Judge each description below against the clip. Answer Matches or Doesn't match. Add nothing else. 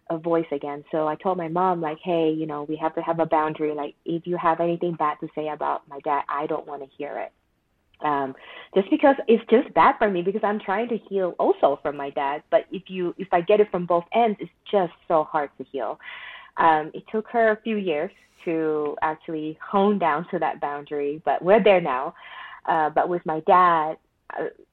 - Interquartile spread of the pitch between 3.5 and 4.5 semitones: Matches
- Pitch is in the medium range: Matches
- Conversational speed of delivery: Doesn't match